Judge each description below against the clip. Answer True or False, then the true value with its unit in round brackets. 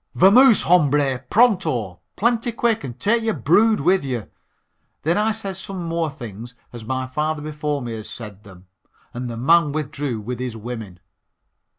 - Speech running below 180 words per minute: True (165 wpm)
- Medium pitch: True (145 Hz)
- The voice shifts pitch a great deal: True (7.8 semitones)